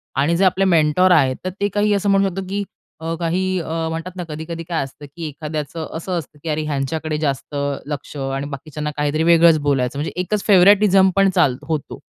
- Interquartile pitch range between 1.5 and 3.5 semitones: No, average, 3.9 semitones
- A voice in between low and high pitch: Yes, medium, 160 Hz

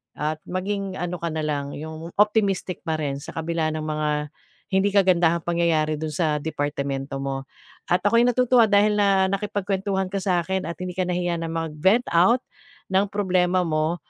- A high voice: No, medium, 175 Hz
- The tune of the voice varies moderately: Yes, average, 3.8 semitones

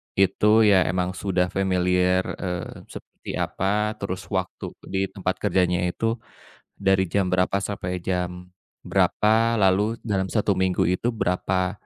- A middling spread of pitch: No, narrow, 1.8 semitones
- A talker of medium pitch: No, very low, 95 Hz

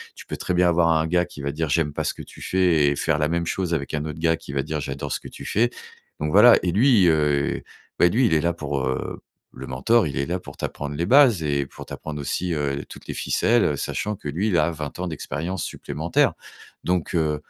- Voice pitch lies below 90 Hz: Yes, very low, 80 Hz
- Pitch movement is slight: No, average, 3.6 semitones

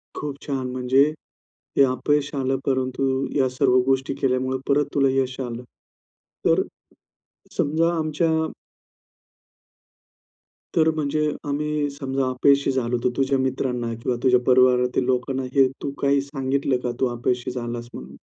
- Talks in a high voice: No, low, 130 Hz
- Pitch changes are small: Yes, narrow, 1.8 semitones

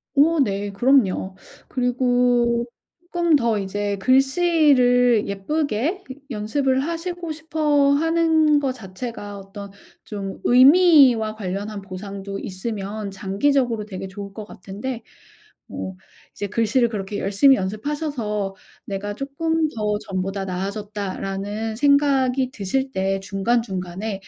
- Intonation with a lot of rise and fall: Yes, wide, 5.7 semitones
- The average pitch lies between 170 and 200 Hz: No, high, 220 Hz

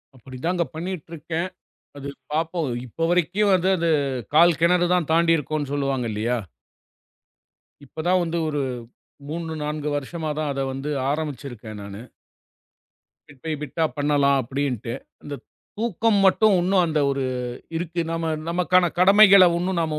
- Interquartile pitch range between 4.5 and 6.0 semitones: No, average, 3.8 semitones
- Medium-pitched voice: Yes, medium, 160 Hz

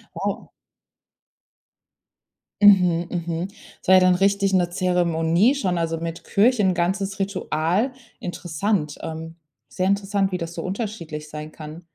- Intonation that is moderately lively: Yes, average, 3.1 semitones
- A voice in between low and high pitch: Yes, medium, 180 Hz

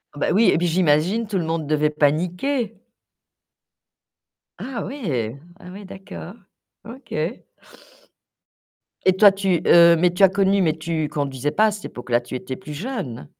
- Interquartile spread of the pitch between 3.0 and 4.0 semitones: No, average, 5.0 semitones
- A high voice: No, medium, 175 Hz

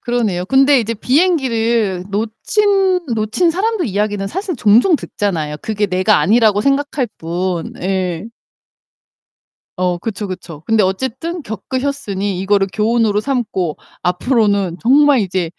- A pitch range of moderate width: No, wide, 6.0 semitones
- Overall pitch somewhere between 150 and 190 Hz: No, high, 215 Hz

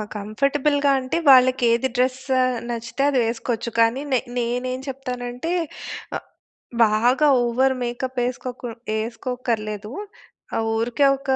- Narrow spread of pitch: Yes, narrow, 2.0 semitones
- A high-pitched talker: Yes, very high, 250 Hz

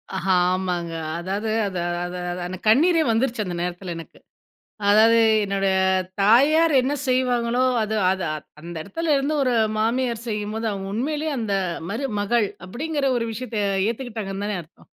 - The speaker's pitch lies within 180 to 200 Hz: No, high, 220 Hz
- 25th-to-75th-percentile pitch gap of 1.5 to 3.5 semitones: No, average, 4.7 semitones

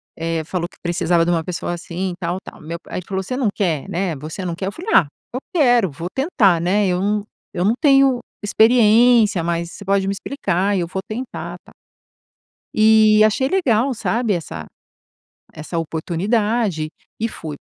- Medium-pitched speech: No, high, 195 Hz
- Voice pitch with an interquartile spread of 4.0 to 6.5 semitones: Yes, average, 4.7 semitones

